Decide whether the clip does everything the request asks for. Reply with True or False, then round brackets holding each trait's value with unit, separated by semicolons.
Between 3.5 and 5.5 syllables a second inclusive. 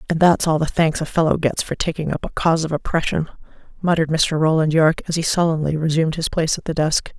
False (6.7 syllables/s)